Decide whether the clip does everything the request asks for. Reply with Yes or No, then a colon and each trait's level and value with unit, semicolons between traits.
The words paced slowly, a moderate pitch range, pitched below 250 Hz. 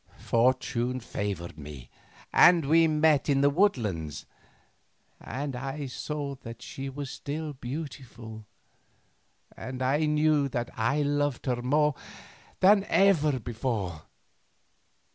Yes: slow, 105 wpm; average, 4.3 semitones; low, 135 Hz